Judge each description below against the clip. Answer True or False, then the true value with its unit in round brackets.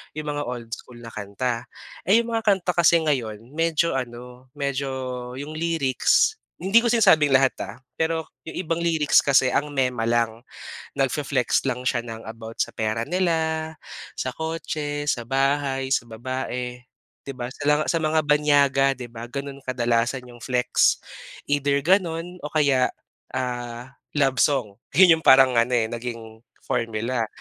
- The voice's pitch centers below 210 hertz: True (135 Hz)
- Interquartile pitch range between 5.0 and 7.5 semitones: False (4.2 semitones)